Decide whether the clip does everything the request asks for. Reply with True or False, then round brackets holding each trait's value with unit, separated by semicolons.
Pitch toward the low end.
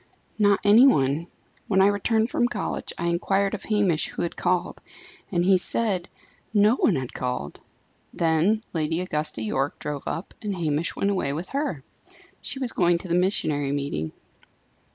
False (175 Hz)